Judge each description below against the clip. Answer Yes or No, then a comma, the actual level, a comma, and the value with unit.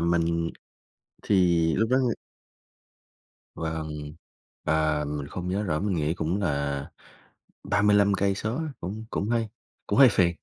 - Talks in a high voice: No, very low, 85 Hz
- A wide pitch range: No, average, 4.4 semitones